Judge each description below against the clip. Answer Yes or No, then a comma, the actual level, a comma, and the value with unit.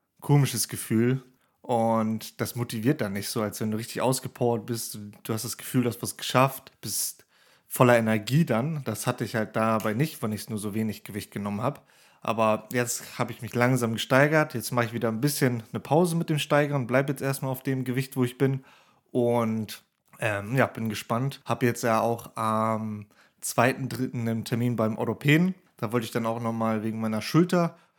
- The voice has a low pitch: Yes, low, 120 Hz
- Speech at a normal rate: No, fast, 200 wpm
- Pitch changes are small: No, average, 3.0 semitones